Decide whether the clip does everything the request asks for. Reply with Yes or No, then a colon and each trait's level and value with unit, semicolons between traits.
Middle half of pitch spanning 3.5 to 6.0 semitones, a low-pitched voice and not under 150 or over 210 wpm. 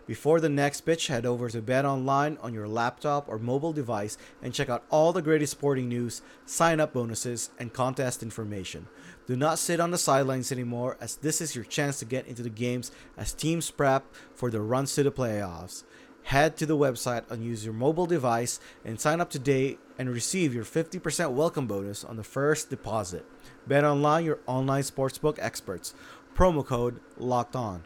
Yes: average, 4.2 semitones; low, 130 Hz; average, 185 wpm